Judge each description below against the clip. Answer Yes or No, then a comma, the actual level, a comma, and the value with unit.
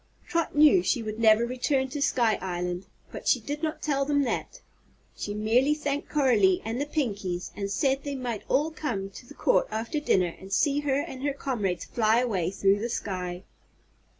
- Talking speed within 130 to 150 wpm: No, average, 190 wpm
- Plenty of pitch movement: Yes, wide, 6.0 semitones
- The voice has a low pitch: No, high, 240 Hz